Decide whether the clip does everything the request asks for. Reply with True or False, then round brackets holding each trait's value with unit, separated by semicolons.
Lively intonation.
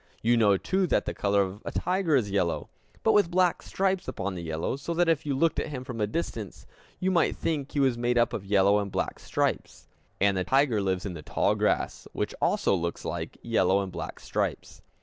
True (8.5 semitones)